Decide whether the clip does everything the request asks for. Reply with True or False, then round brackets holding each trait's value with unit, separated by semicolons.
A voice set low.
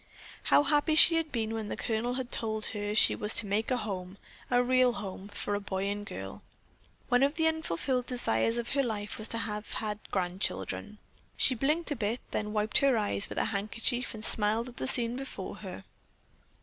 False (220 Hz)